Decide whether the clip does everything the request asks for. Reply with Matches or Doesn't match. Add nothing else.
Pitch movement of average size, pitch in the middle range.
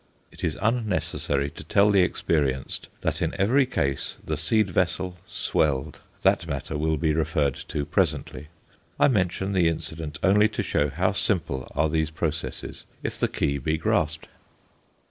Doesn't match